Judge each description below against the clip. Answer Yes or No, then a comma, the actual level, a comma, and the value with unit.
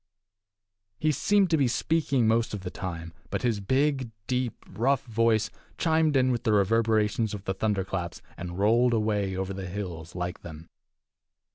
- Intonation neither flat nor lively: Yes, average, 4.8 semitones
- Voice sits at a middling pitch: No, low, 110 Hz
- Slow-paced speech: No, average, 165 wpm